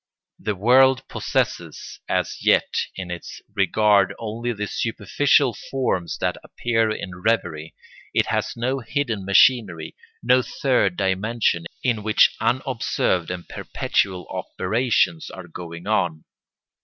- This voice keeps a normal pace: No, slow, 120 wpm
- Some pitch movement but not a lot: Yes, average, 4.9 semitones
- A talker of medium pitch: No, low, 110 Hz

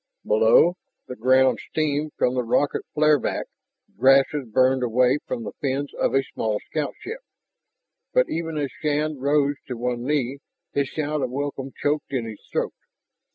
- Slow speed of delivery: No, average, 155 wpm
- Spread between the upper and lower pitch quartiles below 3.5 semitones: Yes, average, 2.8 semitones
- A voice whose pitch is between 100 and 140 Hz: Yes, low, 135 Hz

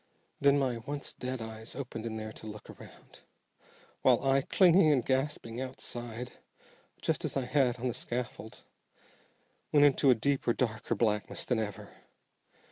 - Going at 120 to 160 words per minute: Yes, average, 150 wpm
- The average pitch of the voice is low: Yes, low, 125 Hz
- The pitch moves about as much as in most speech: Yes, average, 3.5 semitones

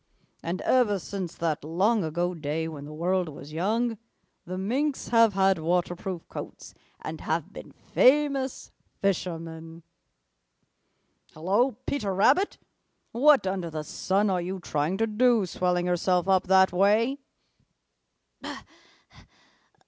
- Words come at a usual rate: No, slow, 120 wpm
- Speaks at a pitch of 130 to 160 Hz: No, high, 190 Hz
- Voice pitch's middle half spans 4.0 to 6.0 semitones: Yes, average, 4.6 semitones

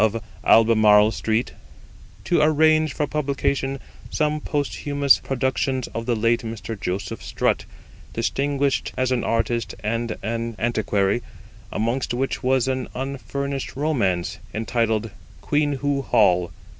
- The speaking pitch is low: Yes, low, 125 Hz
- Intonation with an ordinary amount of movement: Yes, average, 3.8 semitones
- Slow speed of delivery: Yes, slow, 115 wpm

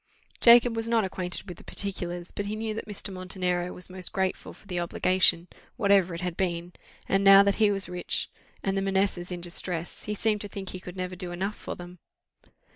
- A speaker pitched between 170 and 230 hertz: Yes, high, 190 Hz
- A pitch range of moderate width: No, narrow, 2.1 semitones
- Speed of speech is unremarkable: No, fast, 210 wpm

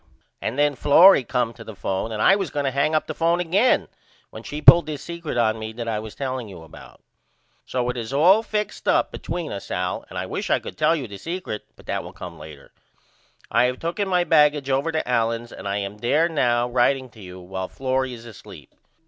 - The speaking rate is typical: No, fast, 230 wpm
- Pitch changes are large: Yes, wide, 6.1 semitones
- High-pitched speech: No, low, 130 Hz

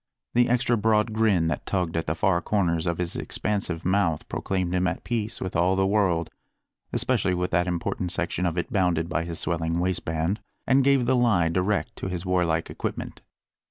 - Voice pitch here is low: Yes, very low, 90 Hz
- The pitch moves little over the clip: No, average, 3.7 semitones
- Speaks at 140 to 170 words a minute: No, average, 190 wpm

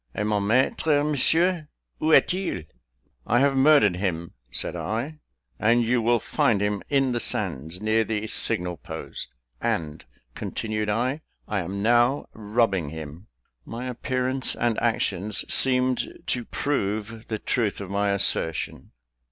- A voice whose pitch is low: Yes, low, 115 Hz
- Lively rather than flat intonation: No, average, 4.3 semitones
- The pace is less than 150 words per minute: Yes, average, 140 wpm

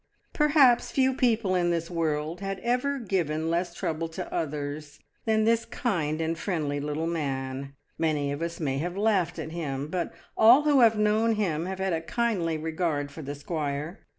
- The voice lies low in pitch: No, medium, 170 Hz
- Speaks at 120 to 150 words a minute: No, average, 180 wpm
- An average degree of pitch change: No, wide, 5.9 semitones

